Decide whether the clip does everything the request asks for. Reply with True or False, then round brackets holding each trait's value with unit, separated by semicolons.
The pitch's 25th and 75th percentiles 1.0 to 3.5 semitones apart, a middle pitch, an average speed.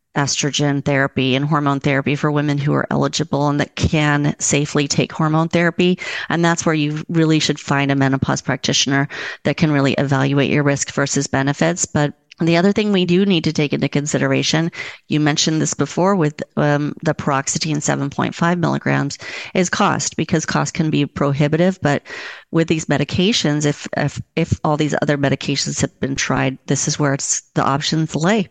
True (2.7 semitones; 150 Hz; 175 wpm)